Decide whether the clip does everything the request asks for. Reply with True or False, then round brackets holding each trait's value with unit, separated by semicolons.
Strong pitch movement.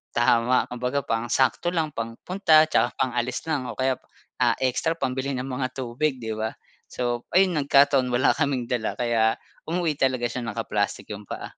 False (2.9 semitones)